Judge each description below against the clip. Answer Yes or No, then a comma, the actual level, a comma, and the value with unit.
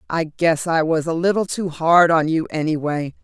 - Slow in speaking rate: No, fast, 205 wpm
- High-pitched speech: No, medium, 165 Hz